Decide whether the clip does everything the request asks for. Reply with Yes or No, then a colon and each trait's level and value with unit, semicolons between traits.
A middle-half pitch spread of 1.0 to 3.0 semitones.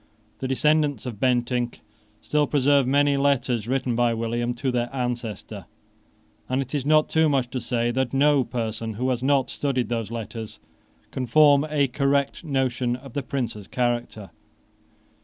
Yes: average, 2.7 semitones